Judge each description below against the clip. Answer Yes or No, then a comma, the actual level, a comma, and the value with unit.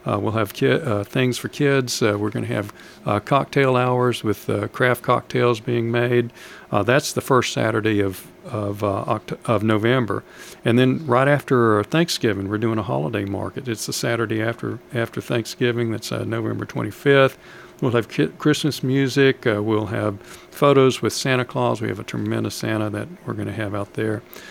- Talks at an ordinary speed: Yes, average, 190 wpm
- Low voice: Yes, low, 115 Hz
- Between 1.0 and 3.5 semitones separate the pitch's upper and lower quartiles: Yes, average, 3.2 semitones